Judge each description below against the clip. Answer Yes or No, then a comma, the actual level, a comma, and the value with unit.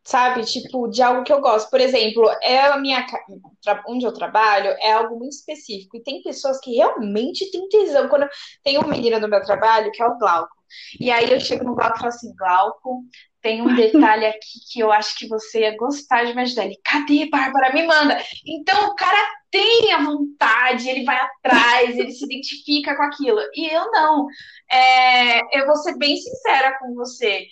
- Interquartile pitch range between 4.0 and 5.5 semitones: Yes, average, 4.3 semitones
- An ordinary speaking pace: No, fast, 200 wpm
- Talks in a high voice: Yes, very high, 255 Hz